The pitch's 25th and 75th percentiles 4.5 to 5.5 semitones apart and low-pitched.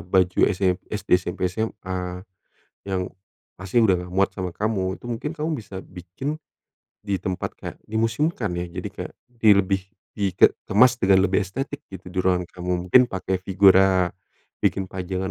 No: average, 2.7 semitones; very low, 95 Hz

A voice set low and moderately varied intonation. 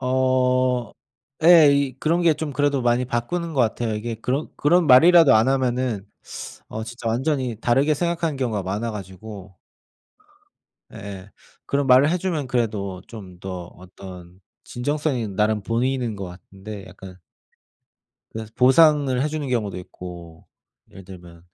No: low, 120 Hz; wide, 5.8 semitones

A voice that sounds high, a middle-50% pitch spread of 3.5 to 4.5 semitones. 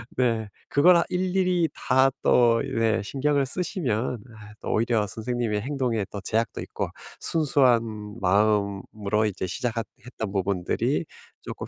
No: low, 115 Hz; average, 4.2 semitones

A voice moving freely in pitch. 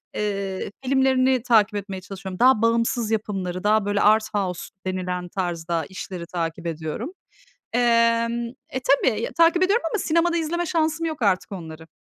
Yes: wide, 5.8 semitones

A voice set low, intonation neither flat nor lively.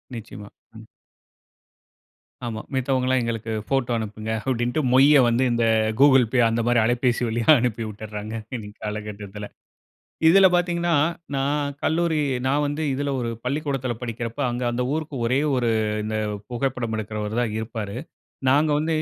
Yes: low, 120 Hz; average, 3.8 semitones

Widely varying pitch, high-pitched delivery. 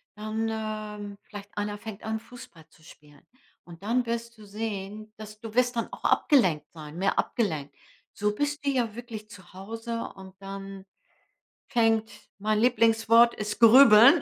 No: average, 2.7 semitones; high, 215 Hz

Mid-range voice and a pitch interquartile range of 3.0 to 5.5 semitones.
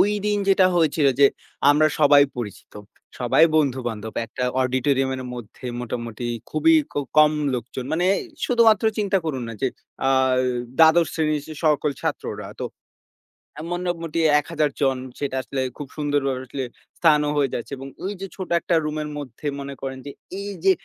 Yes: medium, 145 Hz; average, 3.9 semitones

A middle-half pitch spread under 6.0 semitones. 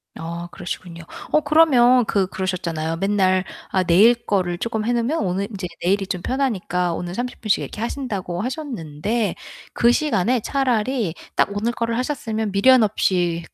Yes: average, 5.2 semitones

